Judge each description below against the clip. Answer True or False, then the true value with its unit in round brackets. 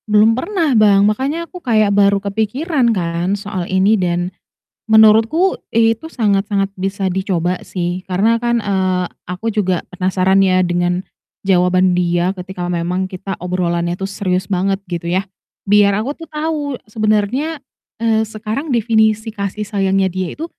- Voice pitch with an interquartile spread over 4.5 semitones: False (3.3 semitones)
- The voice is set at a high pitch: True (200 Hz)